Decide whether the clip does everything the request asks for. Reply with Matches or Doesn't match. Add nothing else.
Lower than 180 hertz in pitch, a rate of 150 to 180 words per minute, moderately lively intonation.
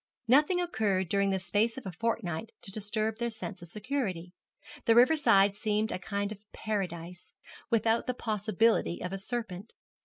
Doesn't match